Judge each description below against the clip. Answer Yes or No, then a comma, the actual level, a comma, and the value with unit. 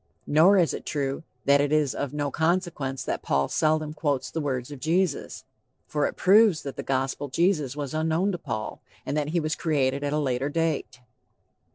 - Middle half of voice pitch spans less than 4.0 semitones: Yes, average, 2.9 semitones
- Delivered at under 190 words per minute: No, average, 195 wpm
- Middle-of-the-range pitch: Yes, medium, 150 Hz